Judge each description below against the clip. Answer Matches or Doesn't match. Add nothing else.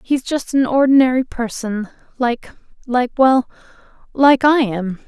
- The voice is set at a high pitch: Matches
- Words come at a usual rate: Doesn't match